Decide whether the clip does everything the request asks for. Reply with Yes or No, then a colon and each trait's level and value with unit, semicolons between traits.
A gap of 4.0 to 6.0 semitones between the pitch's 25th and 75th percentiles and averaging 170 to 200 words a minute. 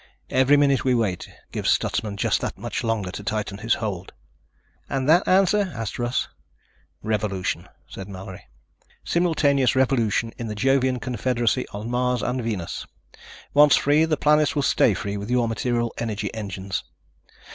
No: average, 4.4 semitones; average, 150 wpm